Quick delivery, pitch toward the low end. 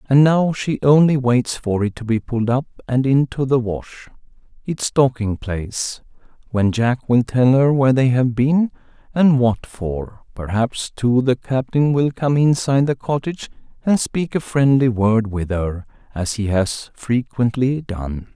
No: average, 165 wpm; low, 125 Hz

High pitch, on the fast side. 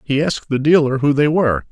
No: medium, 140 Hz; fast, 245 wpm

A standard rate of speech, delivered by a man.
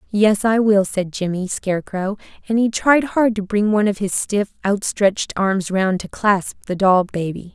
No: average, 190 wpm; female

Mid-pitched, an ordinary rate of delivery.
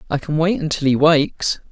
No: medium, 155 Hz; fast, 210 wpm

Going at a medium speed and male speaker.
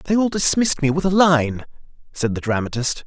Yes: average, 195 wpm; male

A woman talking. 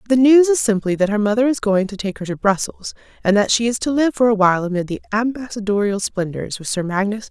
Yes: female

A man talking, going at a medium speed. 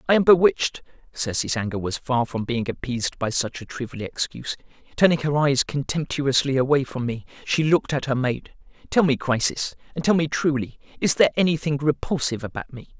Yes: male; average, 185 wpm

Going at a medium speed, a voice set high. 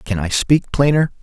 No: average, 195 wpm; low, 125 Hz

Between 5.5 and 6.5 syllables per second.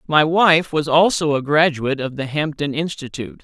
No: 5.2 syllables/s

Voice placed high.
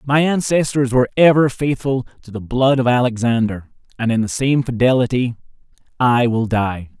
No: low, 125 Hz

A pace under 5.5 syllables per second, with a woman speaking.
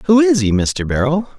No: 5.1 syllables/s; male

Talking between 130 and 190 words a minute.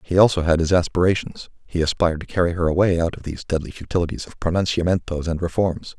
No: average, 200 wpm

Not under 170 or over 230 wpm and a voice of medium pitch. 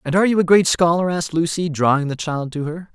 No: fast, 265 wpm; medium, 165 Hz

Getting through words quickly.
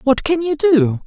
Yes: fast, 225 wpm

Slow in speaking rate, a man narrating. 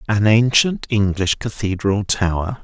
Yes: slow, 115 wpm; male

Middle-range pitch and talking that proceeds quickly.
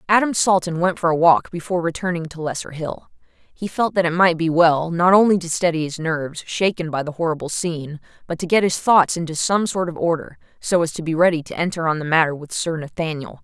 Yes: medium, 170 Hz; fast, 230 wpm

